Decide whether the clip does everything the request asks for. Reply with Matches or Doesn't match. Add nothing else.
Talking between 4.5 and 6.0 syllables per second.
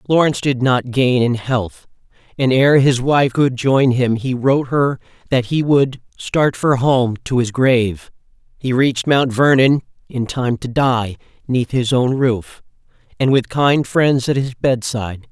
Doesn't match